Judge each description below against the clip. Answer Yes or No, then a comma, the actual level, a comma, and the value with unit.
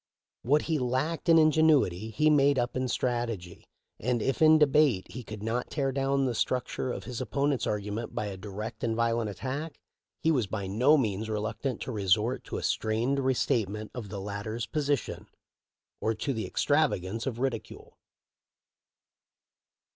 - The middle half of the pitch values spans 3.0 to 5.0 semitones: Yes, average, 4.3 semitones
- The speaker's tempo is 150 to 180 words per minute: Yes, average, 165 wpm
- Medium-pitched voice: No, low, 120 Hz